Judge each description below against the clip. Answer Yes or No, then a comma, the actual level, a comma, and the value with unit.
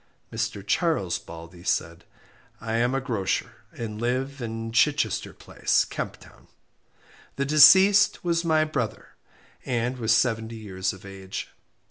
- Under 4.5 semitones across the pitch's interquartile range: No, average, 5.2 semitones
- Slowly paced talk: Yes, slow, 130 wpm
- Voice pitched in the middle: No, low, 115 Hz